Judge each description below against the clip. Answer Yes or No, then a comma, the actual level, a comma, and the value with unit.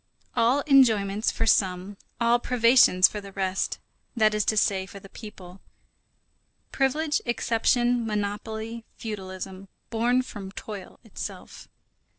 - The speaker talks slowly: Yes, slow, 120 wpm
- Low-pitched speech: No, high, 215 Hz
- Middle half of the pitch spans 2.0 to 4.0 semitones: Yes, average, 3.4 semitones